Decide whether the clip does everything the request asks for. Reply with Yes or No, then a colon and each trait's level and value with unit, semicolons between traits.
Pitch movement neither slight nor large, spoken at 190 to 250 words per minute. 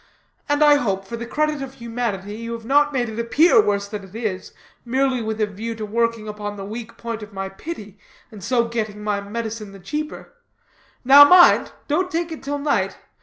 Yes: average, 4.7 semitones; fast, 205 wpm